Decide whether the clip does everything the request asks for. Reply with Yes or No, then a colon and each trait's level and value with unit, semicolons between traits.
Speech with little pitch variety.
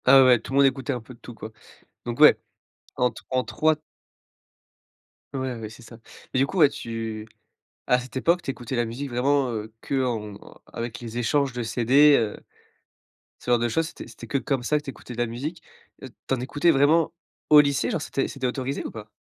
No: average, 3.1 semitones